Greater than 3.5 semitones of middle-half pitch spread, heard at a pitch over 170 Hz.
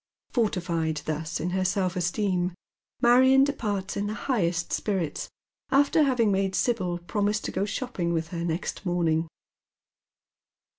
Yes: average, 4.2 semitones; high, 190 Hz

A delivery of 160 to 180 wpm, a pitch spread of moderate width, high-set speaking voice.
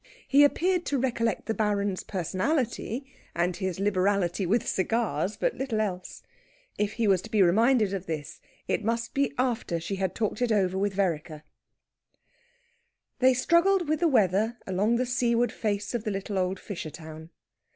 Yes: average, 165 wpm; average, 4.4 semitones; high, 210 Hz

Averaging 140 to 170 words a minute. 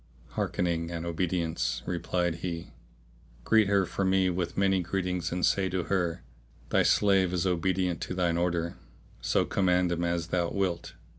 Yes: average, 155 wpm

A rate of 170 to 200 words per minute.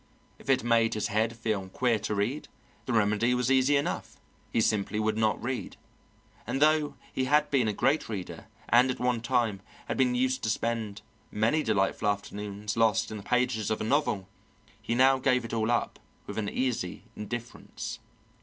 Yes: average, 180 wpm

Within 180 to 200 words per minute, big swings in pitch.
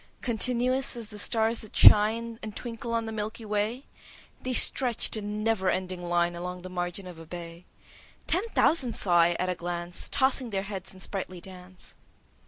No: average, 185 wpm; average, 4.3 semitones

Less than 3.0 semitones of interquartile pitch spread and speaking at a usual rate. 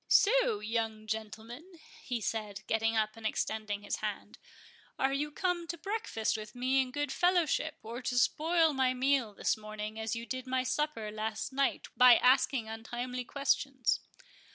No: average, 4.3 semitones; average, 160 wpm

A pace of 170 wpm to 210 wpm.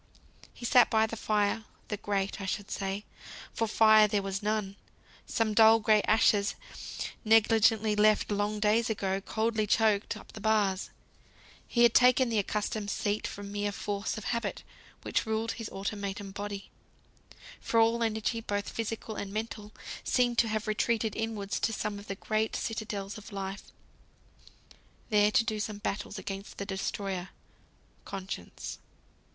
No: average, 150 wpm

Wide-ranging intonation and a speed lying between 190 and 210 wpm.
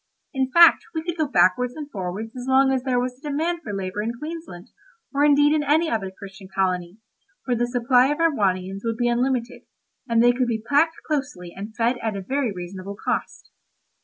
Yes: wide, 6.2 semitones; average, 200 wpm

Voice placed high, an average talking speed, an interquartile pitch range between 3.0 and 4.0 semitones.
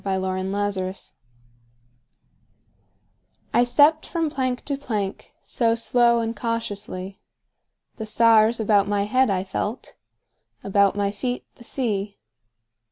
No: high, 210 Hz; slow, 105 wpm; average, 3.4 semitones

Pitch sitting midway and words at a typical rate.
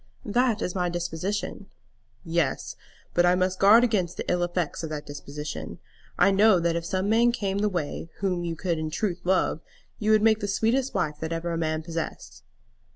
Yes: medium, 180 Hz; average, 195 wpm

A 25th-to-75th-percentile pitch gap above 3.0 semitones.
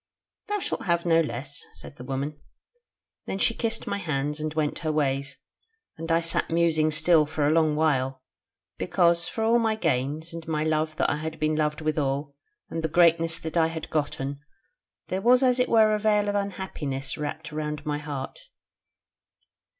No: narrow, 2.5 semitones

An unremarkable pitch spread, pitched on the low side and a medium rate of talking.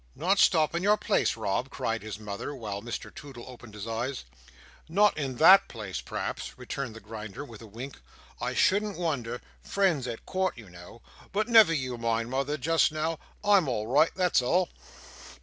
No: wide, 6.7 semitones; low, 130 Hz; average, 170 wpm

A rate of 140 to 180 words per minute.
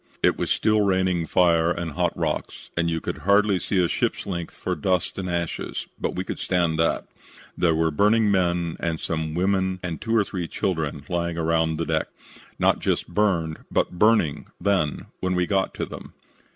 No: average, 190 wpm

